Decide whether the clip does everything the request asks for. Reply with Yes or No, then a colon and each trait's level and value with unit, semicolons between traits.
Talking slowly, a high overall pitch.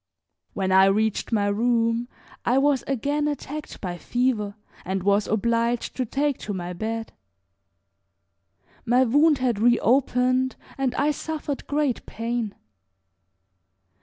Yes: slow, 120 wpm; high, 240 Hz